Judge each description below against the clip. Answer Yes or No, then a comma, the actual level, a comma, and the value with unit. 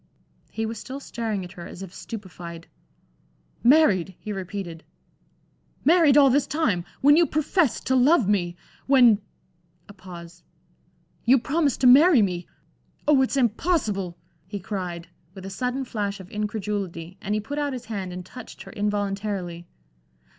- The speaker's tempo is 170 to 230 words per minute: No, average, 150 wpm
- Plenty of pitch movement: Yes, wide, 6.0 semitones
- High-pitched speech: Yes, high, 210 Hz